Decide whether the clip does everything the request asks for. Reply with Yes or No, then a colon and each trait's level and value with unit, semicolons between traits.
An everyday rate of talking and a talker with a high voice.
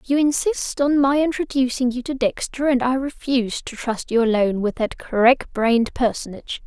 Yes: average, 180 wpm; very high, 255 Hz